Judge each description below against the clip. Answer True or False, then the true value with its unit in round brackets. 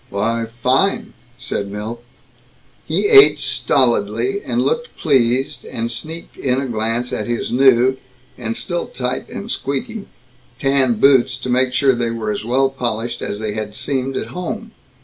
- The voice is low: True (125 Hz)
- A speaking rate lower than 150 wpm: False (165 wpm)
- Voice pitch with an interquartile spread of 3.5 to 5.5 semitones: False (3.0 semitones)